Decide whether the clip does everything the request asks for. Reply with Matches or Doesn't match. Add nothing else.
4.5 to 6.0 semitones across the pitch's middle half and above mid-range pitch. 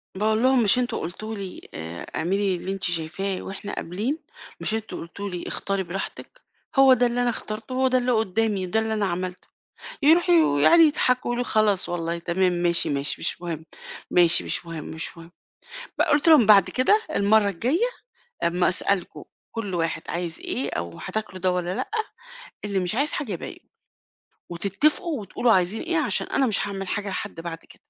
Matches